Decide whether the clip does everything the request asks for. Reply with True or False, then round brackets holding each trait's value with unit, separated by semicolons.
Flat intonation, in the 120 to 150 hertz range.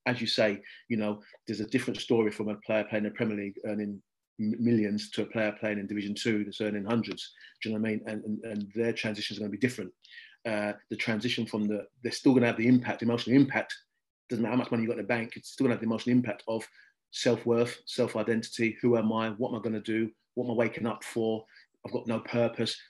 False (1.9 semitones; 110 Hz)